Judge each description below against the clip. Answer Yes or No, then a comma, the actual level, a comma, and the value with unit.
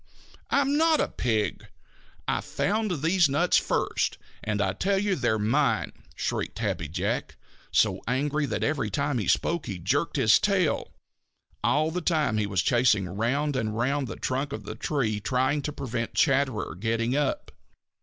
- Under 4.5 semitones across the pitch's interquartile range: No, wide, 5.6 semitones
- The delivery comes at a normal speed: Yes, average, 165 wpm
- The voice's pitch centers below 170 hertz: Yes, low, 135 Hz